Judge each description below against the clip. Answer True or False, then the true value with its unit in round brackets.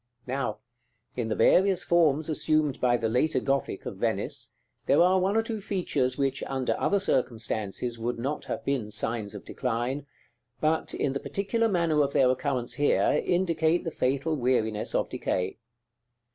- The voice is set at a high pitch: False (140 Hz)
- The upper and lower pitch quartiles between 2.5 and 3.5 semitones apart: False (5.2 semitones)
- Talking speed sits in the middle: True (160 wpm)